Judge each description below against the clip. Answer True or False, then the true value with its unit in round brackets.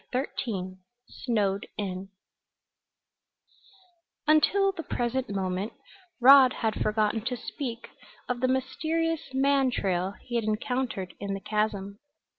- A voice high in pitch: True (235 Hz)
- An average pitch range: True (4.8 semitones)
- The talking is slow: True (115 wpm)